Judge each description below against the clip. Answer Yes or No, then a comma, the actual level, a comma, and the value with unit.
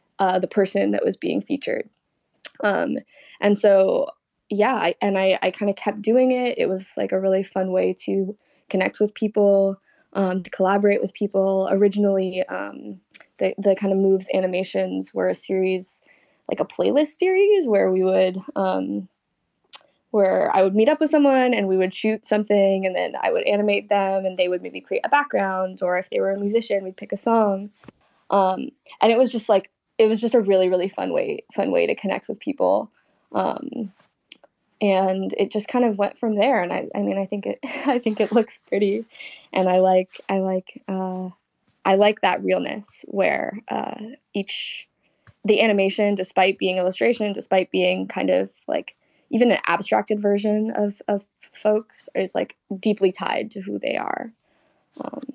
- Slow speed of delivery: No, average, 185 wpm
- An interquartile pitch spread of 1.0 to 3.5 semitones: Yes, average, 3.0 semitones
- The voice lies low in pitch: No, high, 200 Hz